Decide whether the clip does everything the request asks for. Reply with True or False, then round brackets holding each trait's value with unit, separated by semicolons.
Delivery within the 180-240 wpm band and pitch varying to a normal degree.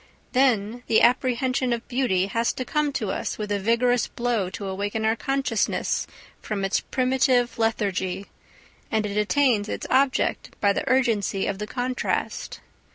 False (155 wpm; 3.8 semitones)